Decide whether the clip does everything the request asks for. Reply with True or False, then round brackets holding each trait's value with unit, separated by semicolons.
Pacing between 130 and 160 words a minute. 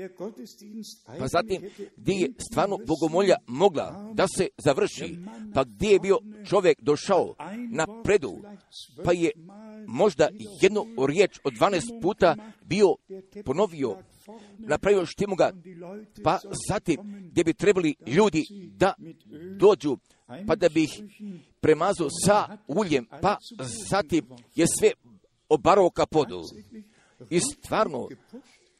False (115 wpm)